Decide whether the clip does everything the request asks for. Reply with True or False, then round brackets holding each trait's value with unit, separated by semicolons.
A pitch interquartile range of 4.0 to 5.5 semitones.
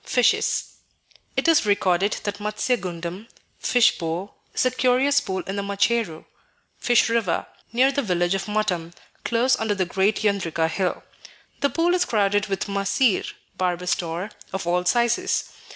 True (4.7 semitones)